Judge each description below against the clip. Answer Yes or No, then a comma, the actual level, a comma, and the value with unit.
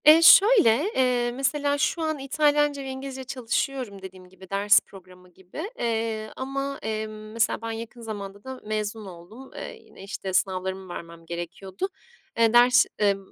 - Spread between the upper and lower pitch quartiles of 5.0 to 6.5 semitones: Yes, wide, 5.6 semitones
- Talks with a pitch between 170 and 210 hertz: No, high, 225 Hz